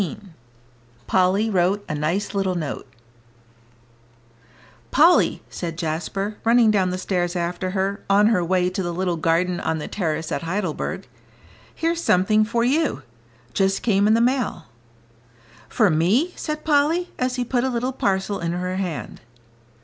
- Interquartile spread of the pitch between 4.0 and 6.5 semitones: Yes, average, 4.6 semitones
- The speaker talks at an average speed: Yes, average, 150 wpm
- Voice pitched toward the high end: Yes, high, 195 Hz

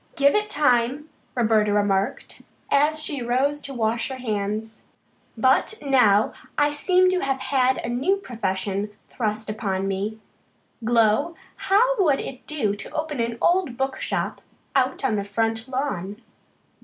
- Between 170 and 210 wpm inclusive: No, average, 145 wpm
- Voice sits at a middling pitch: No, high, 245 Hz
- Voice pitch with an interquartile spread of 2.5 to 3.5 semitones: No, average, 5.1 semitones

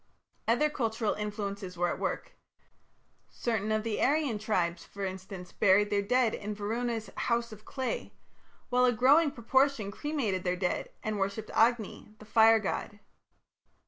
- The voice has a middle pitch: No, high, 215 Hz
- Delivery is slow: No, average, 145 wpm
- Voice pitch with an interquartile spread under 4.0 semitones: Yes, average, 3.3 semitones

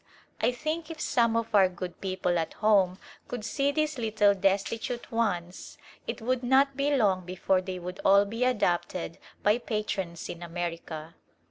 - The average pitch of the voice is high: Yes, high, 205 Hz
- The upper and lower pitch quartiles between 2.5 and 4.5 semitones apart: No, average, 5.1 semitones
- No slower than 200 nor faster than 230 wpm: No, average, 160 wpm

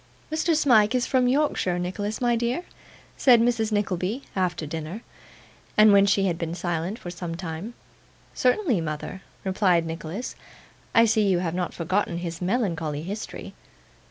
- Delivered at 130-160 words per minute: Yes, average, 150 wpm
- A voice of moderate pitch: No, high, 195 Hz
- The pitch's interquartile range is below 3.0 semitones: No, average, 5.2 semitones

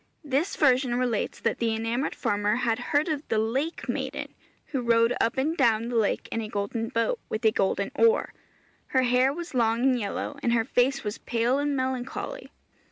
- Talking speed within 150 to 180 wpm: No, average, 190 wpm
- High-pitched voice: Yes, high, 245 Hz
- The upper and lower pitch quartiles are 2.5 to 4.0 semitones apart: Yes, average, 3.2 semitones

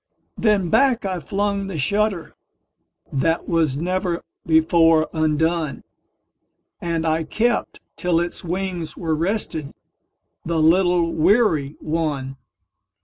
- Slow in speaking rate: Yes, slow, 90 wpm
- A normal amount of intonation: Yes, average, 3.1 semitones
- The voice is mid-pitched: Yes, medium, 165 Hz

